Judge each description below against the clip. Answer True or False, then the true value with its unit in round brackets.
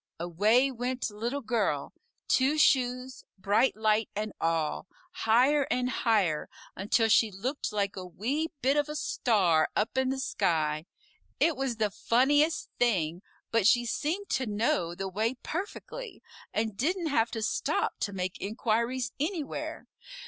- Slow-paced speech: False (145 wpm)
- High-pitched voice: True (230 Hz)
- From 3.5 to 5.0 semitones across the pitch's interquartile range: True (4.7 semitones)